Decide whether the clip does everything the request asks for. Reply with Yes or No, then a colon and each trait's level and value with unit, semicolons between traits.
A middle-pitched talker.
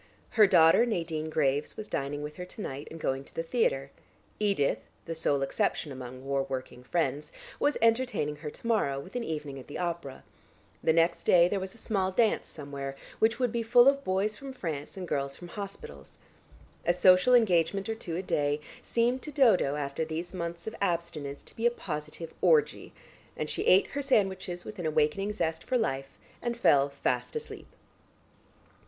Yes: medium, 170 Hz